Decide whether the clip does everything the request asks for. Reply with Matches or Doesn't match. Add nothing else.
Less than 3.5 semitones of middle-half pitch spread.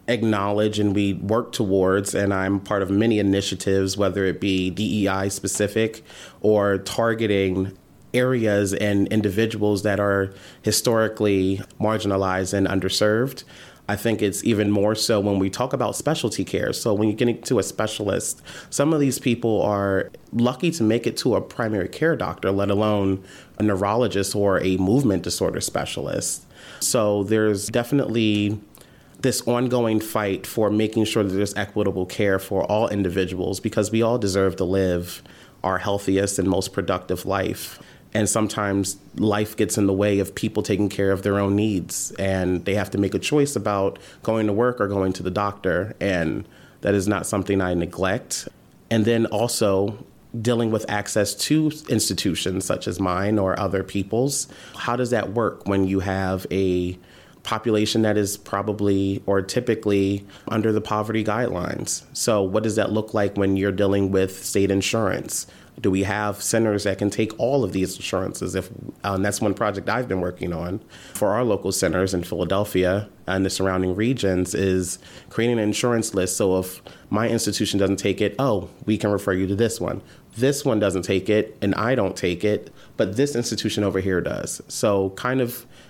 Matches